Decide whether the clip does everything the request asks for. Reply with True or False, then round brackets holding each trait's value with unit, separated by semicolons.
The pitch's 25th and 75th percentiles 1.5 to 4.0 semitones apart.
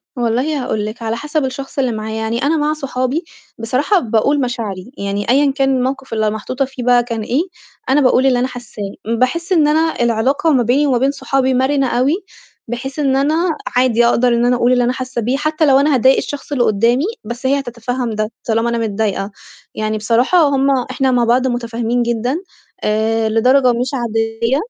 True (3.0 semitones)